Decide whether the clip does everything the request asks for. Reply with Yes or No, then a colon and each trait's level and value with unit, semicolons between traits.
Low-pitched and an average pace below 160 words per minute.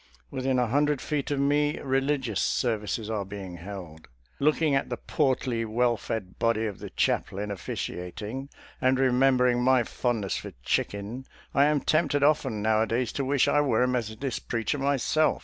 No: low, 125 Hz; average, 165 wpm